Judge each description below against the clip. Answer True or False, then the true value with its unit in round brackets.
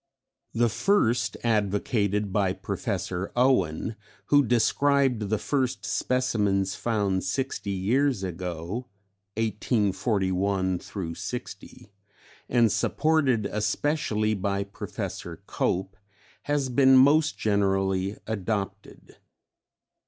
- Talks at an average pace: False (85 wpm)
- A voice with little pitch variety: False (4.5 semitones)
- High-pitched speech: False (105 Hz)